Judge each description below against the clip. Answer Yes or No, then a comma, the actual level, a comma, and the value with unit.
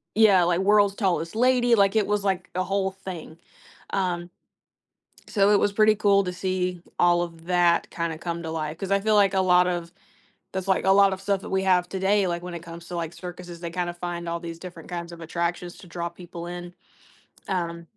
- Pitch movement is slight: Yes, narrow, 2.3 semitones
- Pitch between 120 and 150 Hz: No, medium, 180 Hz